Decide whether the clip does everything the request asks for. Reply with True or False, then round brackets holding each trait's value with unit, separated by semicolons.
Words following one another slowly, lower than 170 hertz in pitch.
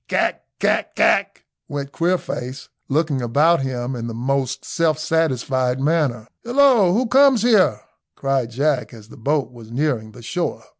False (150 wpm; 135 Hz)